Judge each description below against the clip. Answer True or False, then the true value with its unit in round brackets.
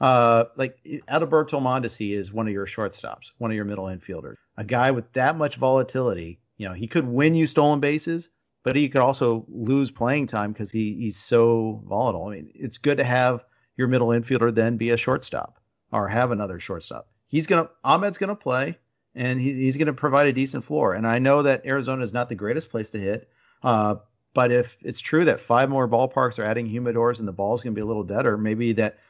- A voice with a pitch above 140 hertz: False (120 Hz)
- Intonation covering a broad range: False (3.4 semitones)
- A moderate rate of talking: False (225 wpm)